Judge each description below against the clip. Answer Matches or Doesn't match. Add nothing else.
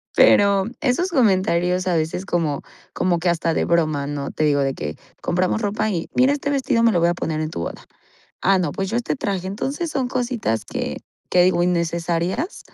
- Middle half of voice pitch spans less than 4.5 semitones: Doesn't match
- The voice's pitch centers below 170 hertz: Doesn't match